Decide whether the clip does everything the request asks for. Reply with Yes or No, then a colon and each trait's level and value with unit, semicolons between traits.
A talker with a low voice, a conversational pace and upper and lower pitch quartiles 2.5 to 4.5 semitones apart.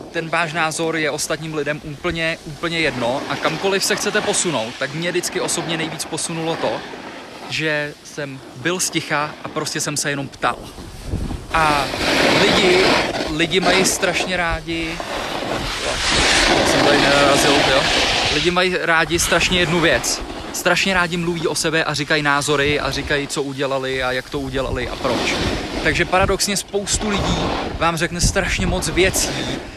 No: medium, 160 Hz; average, 145 wpm; average, 2.8 semitones